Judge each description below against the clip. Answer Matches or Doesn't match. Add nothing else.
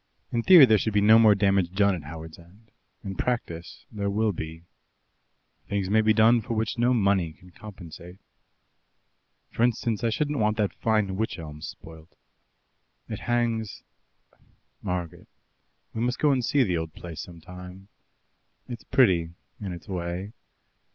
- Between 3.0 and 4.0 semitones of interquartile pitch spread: Doesn't match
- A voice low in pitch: Matches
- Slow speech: Doesn't match